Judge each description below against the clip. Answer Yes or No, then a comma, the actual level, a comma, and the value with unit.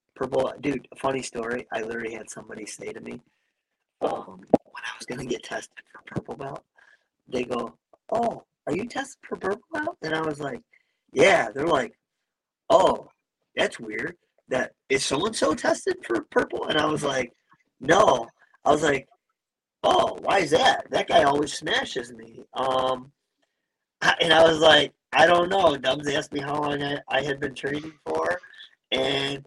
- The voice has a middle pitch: Yes, medium, 150 Hz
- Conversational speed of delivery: Yes, average, 175 wpm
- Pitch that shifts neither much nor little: No, wide, 8.9 semitones